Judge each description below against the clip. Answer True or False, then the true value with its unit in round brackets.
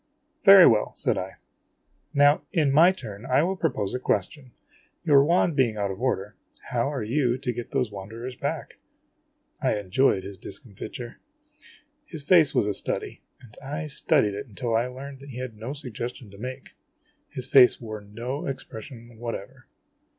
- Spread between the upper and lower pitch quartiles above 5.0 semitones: False (4.5 semitones)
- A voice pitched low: True (125 Hz)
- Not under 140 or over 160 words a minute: False (180 wpm)